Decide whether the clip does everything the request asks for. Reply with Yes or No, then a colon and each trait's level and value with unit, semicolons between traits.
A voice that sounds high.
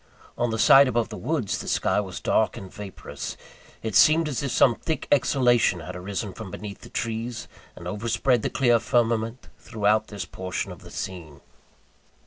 No: low, 110 Hz